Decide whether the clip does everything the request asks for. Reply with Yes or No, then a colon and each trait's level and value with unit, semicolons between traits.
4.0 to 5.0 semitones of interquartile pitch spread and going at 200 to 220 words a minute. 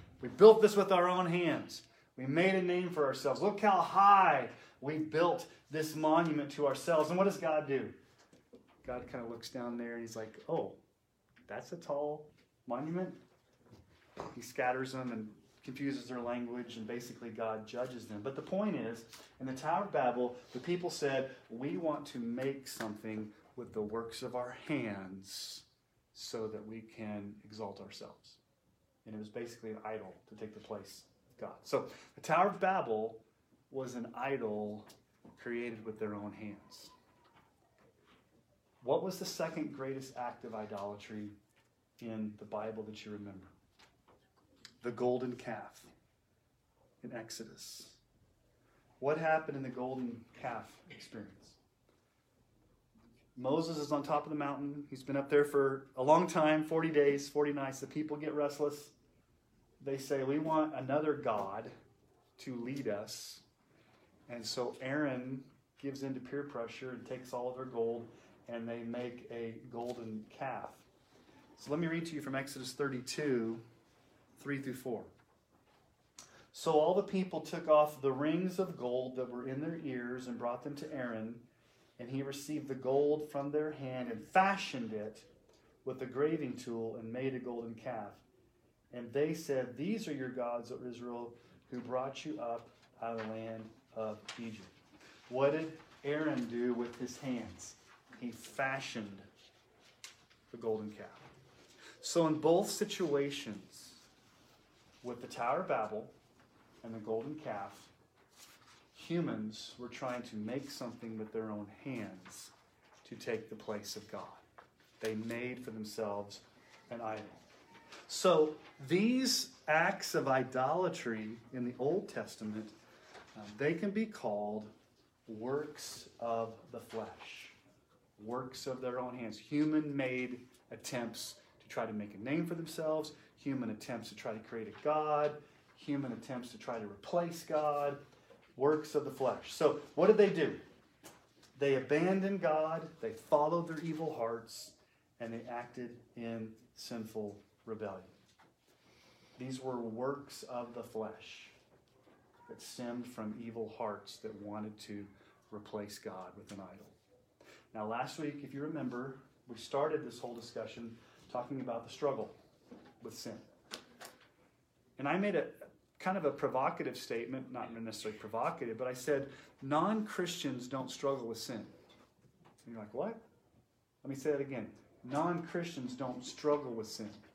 No: average, 4.5 semitones; average, 150 wpm